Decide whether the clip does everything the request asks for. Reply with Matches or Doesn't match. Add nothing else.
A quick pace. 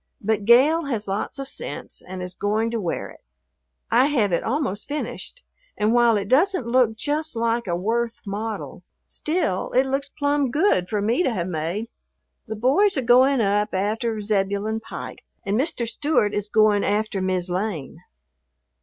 Doesn't match